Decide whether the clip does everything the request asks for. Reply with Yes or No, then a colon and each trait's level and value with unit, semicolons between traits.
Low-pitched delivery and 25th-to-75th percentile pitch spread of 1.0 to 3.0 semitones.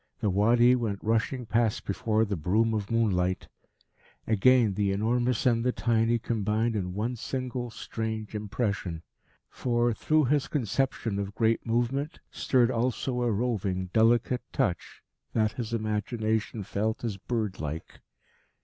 Yes: low, 110 Hz; average, 2.7 semitones